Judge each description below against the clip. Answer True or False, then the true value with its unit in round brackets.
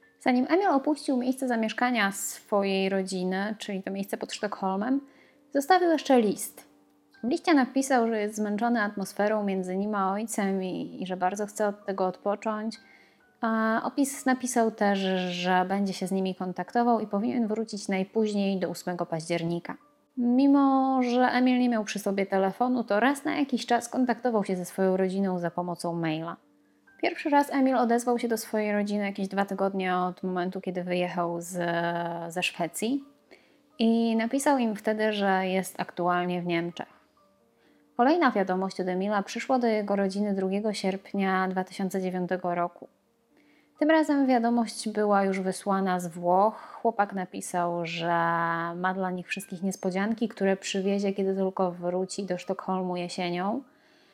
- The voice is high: True (200 Hz)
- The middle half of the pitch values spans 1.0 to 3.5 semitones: False (4.2 semitones)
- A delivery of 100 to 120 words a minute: False (150 wpm)